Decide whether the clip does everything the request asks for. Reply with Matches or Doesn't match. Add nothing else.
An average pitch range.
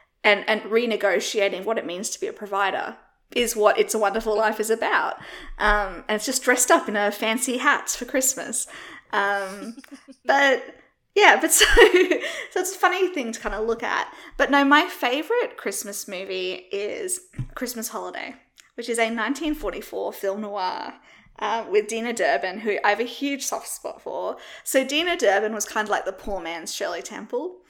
Doesn't match